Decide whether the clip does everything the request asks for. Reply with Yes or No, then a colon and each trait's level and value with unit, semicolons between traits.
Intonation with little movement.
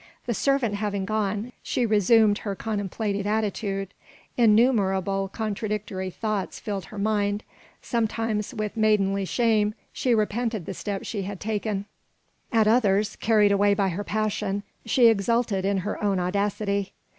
Yes: narrow, 1.8 semitones